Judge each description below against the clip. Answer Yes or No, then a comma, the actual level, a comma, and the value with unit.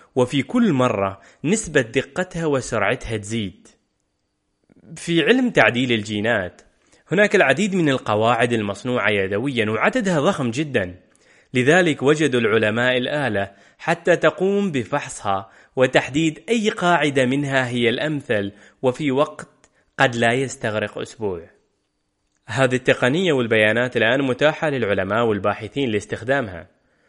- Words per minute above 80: Yes, average, 105 wpm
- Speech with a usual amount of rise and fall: No, wide, 5.9 semitones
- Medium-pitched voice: No, low, 130 Hz